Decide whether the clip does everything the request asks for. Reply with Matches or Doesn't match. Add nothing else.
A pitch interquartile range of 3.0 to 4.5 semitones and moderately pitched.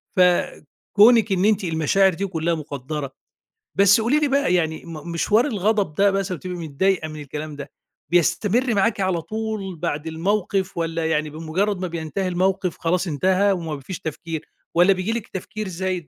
Matches